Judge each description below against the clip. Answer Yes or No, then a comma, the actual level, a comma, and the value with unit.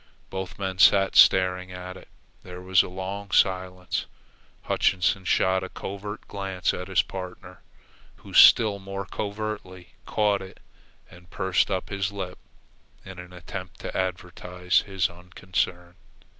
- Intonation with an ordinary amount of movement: No, narrow, 1.2 semitones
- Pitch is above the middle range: No, very low, 95 Hz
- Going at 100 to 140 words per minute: Yes, slow, 135 wpm